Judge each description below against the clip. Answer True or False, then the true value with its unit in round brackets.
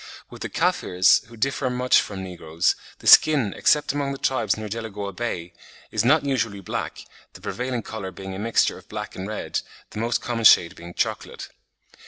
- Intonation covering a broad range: False (4.6 semitones)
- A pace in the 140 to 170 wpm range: False (185 wpm)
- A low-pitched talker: True (110 Hz)